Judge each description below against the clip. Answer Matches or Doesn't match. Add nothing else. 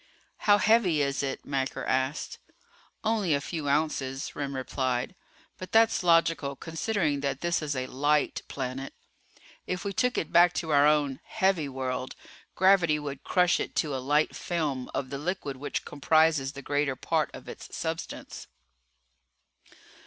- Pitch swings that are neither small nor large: Matches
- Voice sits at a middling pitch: Matches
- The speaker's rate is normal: Matches